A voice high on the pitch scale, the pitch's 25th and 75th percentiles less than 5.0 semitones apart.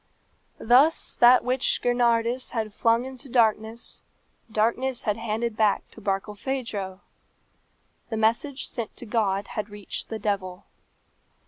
Yes: high, 225 Hz; narrow, 2.6 semitones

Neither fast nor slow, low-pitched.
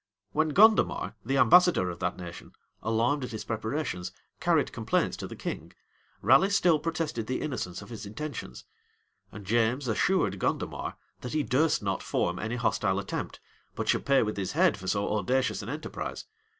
Yes: average, 170 wpm; low, 120 Hz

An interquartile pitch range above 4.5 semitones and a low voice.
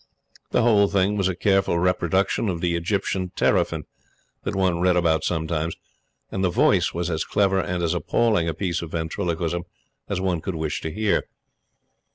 No: narrow, 2.5 semitones; very low, 90 Hz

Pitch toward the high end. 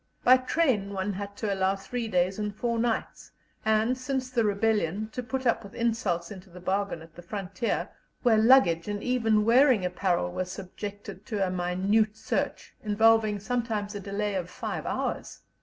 Yes: high, 210 Hz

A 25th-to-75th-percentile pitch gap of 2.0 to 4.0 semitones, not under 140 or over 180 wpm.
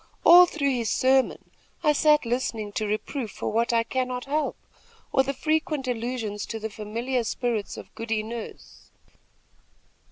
Yes: average, 3.5 semitones; average, 150 wpm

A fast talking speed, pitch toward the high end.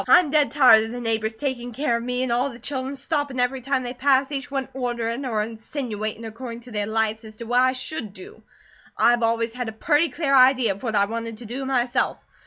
Yes: fast, 235 wpm; high, 245 Hz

